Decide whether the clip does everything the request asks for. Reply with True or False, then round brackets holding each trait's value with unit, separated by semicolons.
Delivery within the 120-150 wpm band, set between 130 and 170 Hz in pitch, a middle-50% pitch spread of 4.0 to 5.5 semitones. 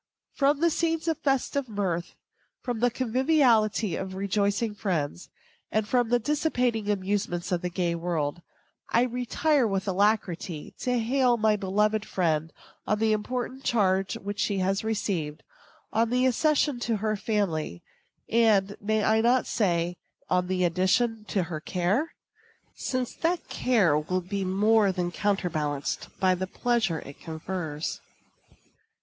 False (140 wpm; 205 Hz; 4.8 semitones)